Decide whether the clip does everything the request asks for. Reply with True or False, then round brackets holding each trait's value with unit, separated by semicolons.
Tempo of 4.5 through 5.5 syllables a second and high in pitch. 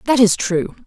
True (4.6 syllables/s; 210 Hz)